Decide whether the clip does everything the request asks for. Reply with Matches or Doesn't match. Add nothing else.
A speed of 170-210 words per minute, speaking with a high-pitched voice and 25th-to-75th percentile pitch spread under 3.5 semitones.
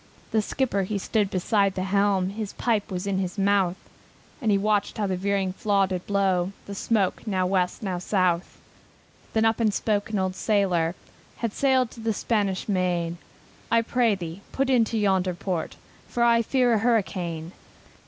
Matches